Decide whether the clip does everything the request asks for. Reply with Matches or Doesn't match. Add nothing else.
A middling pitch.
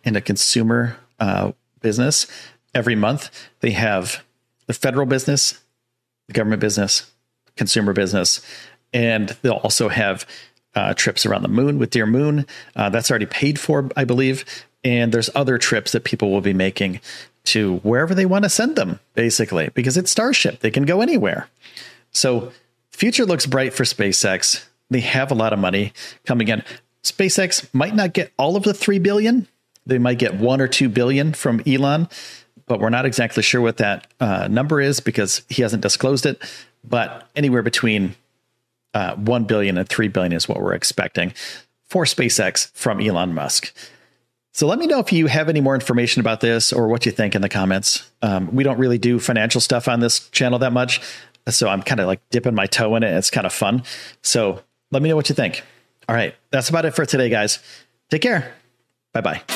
Doesn't match